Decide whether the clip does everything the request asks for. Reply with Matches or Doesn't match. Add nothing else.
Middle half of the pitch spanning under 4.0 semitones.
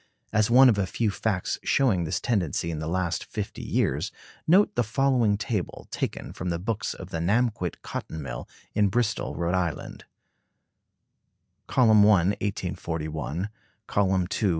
Doesn't match